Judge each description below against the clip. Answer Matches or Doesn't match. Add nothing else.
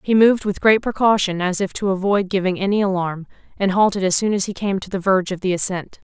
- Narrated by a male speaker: Doesn't match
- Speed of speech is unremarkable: Doesn't match